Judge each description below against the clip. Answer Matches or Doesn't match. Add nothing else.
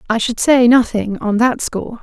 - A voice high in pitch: Matches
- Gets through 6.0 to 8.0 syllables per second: Doesn't match